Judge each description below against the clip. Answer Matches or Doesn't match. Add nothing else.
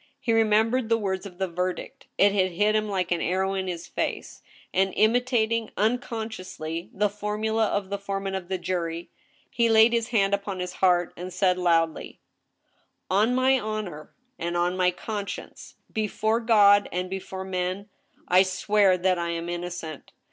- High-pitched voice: Matches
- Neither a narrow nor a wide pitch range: Matches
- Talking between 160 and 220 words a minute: Matches